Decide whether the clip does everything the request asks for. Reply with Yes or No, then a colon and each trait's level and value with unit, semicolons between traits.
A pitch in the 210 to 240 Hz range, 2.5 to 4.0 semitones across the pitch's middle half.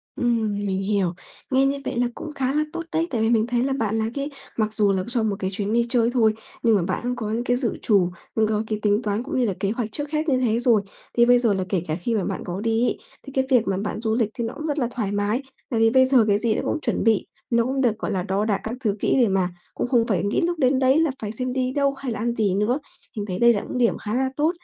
Yes: high, 230 Hz; average, 3.5 semitones